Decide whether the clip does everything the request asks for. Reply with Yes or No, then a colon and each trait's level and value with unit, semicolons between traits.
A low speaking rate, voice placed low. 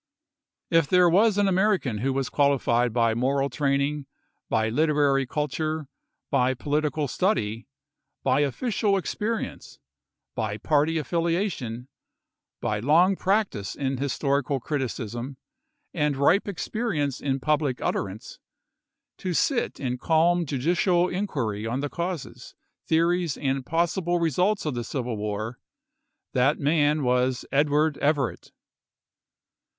No: slow, 115 wpm; medium, 145 Hz